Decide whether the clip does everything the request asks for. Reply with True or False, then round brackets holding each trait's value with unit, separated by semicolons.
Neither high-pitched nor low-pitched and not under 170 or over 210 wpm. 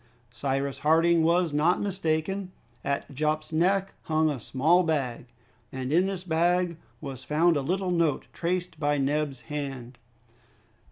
False (155 Hz; 135 wpm)